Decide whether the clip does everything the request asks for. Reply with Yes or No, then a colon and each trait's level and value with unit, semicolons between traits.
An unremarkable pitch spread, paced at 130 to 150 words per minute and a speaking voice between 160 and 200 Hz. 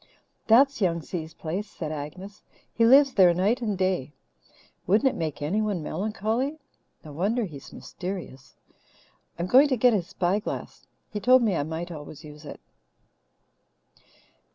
No: wide, 5.8 semitones; average, 145 wpm; high, 190 Hz